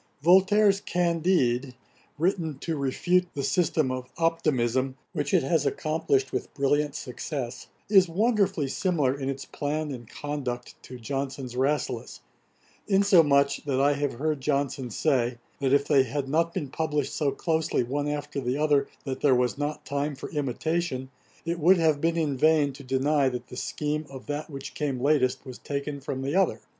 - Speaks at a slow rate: No, average, 170 wpm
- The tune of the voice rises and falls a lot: No, average, 3.1 semitones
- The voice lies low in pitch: No, medium, 145 Hz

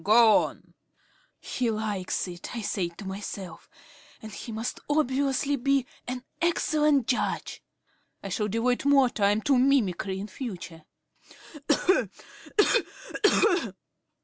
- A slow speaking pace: Yes, slow, 110 wpm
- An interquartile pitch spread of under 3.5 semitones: No, average, 5.2 semitones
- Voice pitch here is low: No, high, 230 Hz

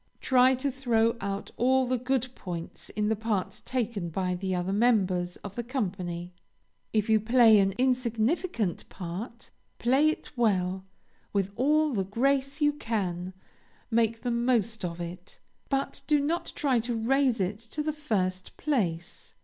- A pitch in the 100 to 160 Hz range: No, high, 225 Hz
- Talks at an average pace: Yes, average, 155 wpm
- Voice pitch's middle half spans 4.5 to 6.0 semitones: Yes, average, 5.2 semitones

